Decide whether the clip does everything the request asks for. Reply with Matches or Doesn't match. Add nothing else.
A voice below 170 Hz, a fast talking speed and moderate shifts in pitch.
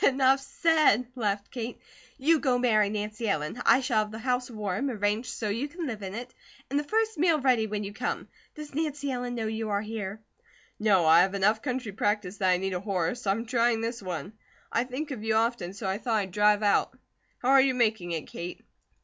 Doesn't match